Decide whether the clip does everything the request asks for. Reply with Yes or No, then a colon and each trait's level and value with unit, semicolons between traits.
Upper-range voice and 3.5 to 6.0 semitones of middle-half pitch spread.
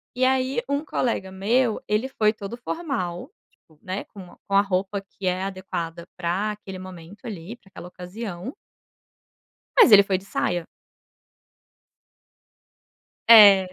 Yes: high, 195 Hz; average, 3.9 semitones